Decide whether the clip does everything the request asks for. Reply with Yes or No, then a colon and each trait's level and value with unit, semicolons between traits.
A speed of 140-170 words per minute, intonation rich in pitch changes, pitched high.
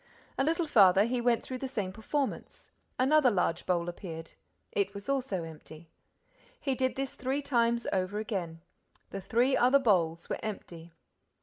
Yes: average, 160 wpm; wide, 6.4 semitones; high, 220 Hz